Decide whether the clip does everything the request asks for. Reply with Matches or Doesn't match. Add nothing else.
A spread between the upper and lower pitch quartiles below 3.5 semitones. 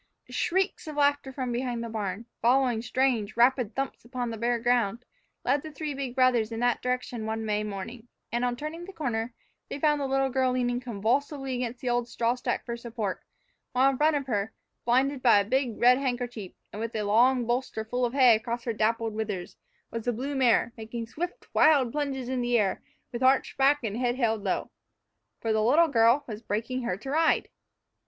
Matches